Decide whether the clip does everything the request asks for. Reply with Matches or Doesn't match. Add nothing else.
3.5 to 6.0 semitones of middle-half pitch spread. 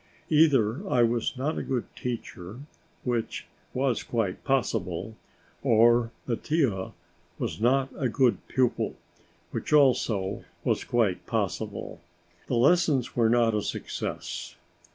Doesn't match